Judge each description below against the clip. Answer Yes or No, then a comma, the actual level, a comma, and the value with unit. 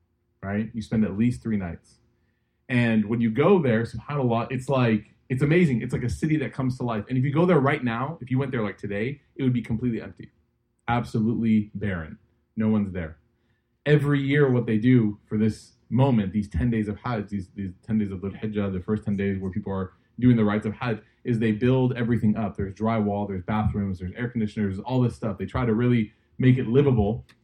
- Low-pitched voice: Yes, low, 115 Hz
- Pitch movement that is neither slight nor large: Yes, average, 3.1 semitones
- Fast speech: Yes, fast, 225 wpm